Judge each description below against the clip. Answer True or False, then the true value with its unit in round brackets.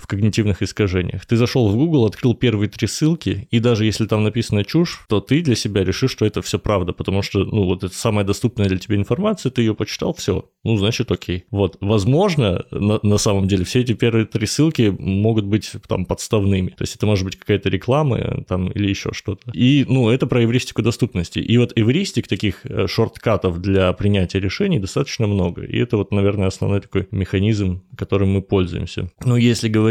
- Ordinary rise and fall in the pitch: True (3.4 semitones)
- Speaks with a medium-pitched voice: False (105 Hz)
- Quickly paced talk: True (195 wpm)